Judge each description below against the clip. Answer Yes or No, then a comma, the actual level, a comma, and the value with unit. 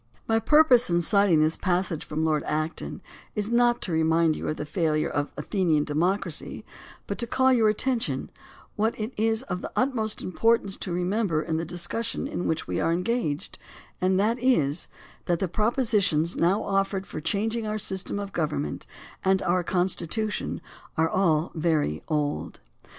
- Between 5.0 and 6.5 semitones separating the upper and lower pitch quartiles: Yes, average, 5.3 semitones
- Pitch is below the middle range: No, medium, 185 Hz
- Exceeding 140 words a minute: Yes, average, 175 wpm